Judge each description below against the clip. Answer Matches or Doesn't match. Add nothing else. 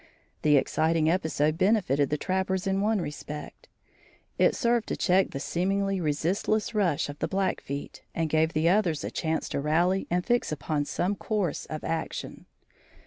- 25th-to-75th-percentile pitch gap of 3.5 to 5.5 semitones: Matches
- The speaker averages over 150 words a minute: Matches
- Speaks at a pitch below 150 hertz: Doesn't match